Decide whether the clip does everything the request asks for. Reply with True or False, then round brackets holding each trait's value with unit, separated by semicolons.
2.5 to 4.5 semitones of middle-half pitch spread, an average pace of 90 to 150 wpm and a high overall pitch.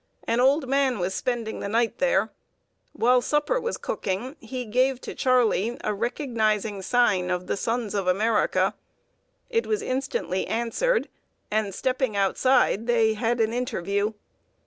True (3.7 semitones; 145 wpm; 235 Hz)